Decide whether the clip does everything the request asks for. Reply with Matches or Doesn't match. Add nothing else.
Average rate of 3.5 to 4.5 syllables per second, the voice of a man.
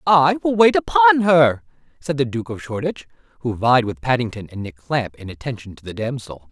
Doesn't match